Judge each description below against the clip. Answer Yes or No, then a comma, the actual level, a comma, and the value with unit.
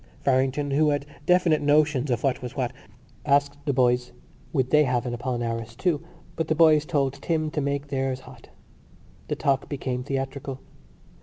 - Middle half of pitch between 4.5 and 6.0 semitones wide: No, narrow, 2.6 semitones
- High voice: No, medium, 140 Hz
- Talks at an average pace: Yes, average, 165 wpm